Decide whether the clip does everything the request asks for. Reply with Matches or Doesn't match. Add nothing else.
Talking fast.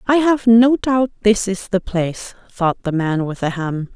Matches